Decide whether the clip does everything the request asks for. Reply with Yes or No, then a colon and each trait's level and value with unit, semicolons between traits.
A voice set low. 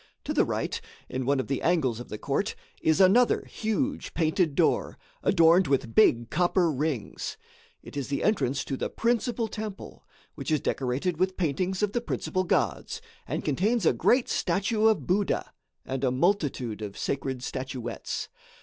No: medium, 165 Hz